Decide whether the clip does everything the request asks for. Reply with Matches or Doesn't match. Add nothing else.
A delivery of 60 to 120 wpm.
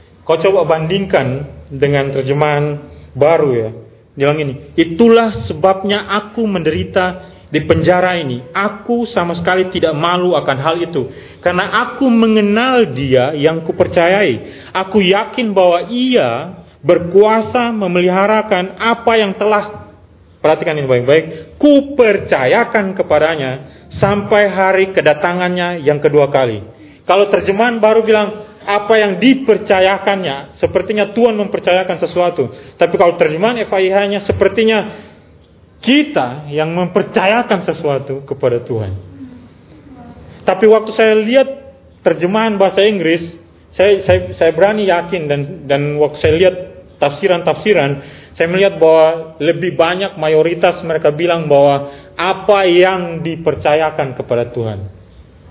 Matches